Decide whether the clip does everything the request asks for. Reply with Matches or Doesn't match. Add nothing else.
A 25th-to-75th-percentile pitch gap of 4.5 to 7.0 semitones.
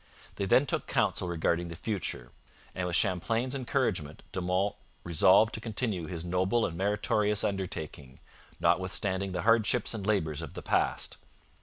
Doesn't match